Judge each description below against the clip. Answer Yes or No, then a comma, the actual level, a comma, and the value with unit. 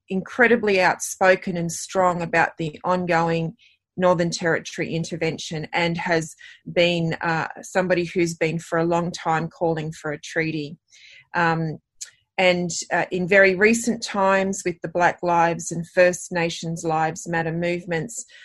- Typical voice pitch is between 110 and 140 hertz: No, medium, 170 Hz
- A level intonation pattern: Yes, narrow, 1.9 semitones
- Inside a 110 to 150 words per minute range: Yes, slow, 135 wpm